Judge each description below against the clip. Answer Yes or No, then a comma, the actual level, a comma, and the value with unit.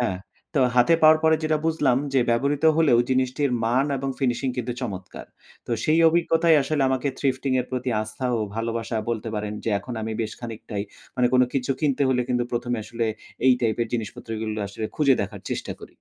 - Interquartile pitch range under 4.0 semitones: Yes, average, 3.3 semitones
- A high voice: No, low, 125 Hz